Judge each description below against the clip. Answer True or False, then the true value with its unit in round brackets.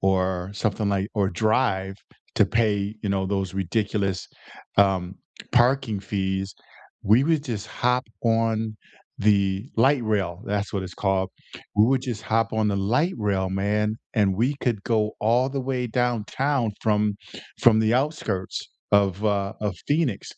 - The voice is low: True (105 Hz)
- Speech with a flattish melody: False (3.4 semitones)